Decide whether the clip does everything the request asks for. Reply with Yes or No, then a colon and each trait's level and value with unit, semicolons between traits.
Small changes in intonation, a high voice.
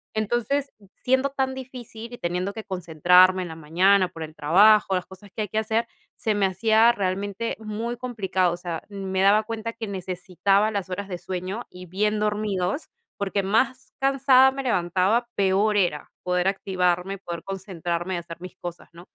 No: average, 3.4 semitones; high, 195 Hz